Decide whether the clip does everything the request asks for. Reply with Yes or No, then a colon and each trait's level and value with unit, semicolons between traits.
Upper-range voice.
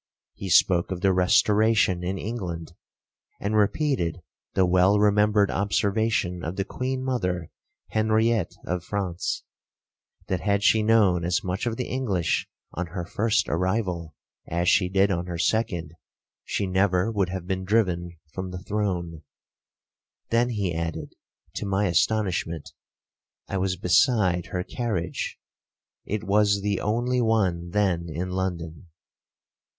No: very low, 95 Hz